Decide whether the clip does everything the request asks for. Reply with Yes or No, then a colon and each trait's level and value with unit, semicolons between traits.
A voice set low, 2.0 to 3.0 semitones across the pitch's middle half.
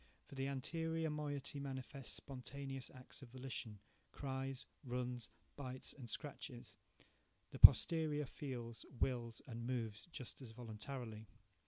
Yes: low, 130 Hz; average, 2.7 semitones